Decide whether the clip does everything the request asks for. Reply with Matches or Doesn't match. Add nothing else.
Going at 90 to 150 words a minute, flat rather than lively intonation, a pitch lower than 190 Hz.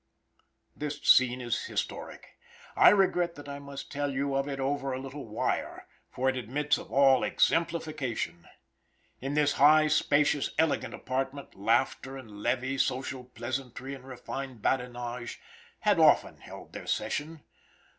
Matches